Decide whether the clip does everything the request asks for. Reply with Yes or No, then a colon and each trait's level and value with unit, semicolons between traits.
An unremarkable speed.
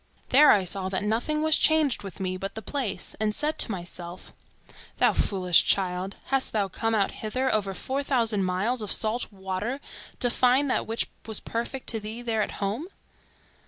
Yes: average, 180 wpm